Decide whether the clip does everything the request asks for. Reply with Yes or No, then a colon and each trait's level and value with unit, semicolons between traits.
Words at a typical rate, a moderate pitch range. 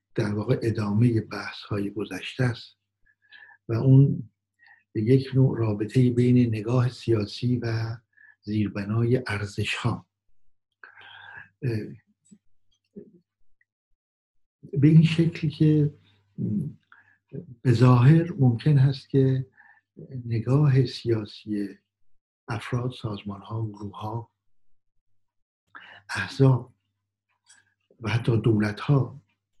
No: slow, 80 wpm; average, 4.5 semitones